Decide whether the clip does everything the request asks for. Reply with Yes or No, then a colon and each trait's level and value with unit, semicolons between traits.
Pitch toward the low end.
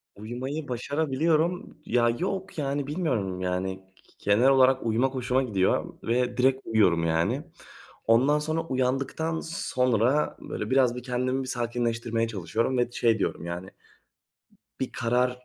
Yes: low, 125 Hz